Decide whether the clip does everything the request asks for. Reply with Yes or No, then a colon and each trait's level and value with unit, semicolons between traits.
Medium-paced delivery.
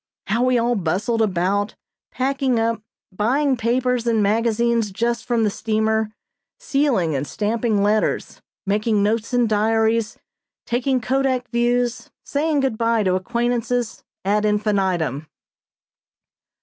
No: slow, 120 wpm